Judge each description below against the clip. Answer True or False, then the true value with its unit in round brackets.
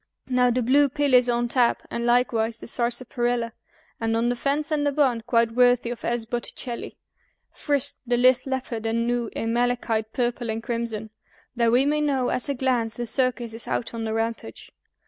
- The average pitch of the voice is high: True (240 Hz)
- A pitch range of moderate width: False (1.7 semitones)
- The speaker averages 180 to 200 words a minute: True (190 wpm)